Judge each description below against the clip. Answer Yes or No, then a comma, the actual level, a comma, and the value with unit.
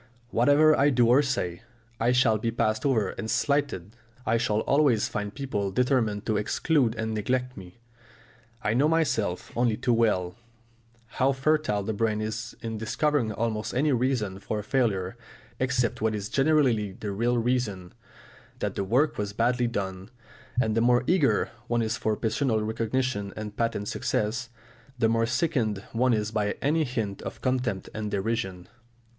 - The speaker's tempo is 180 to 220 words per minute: No, average, 160 wpm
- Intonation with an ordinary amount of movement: Yes, average, 3.3 semitones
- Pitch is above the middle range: No, low, 115 Hz